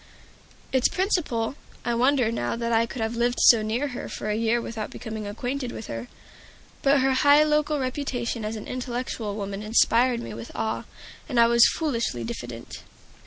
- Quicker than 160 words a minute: Yes, average, 175 wpm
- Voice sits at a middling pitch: No, high, 235 Hz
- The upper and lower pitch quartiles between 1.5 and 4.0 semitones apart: Yes, average, 3.0 semitones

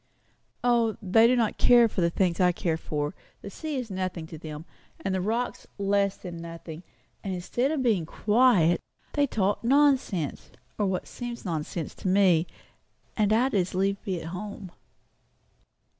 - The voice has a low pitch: No, high, 195 Hz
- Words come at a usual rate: Yes, average, 165 wpm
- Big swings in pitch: No, average, 4.9 semitones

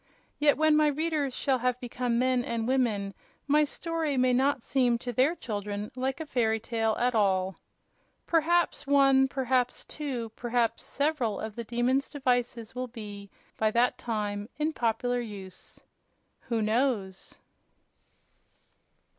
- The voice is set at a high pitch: Yes, high, 245 Hz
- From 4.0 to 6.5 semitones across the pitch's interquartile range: No, average, 3.5 semitones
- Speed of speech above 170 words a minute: No, average, 140 wpm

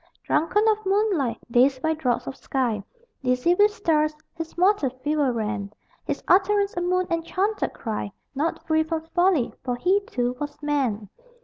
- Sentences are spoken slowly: No, average, 155 wpm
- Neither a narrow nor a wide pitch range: No, wide, 6.5 semitones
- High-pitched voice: Yes, very high, 310 Hz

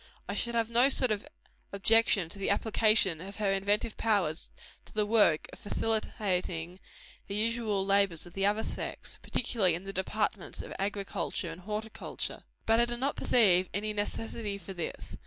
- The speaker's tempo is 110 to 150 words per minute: No, average, 170 wpm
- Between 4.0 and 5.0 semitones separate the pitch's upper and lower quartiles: No, average, 2.7 semitones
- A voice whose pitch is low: No, high, 205 Hz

